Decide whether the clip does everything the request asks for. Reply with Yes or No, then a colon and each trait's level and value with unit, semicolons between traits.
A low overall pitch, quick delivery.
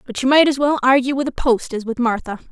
No: very high, 255 Hz; fast, 285 wpm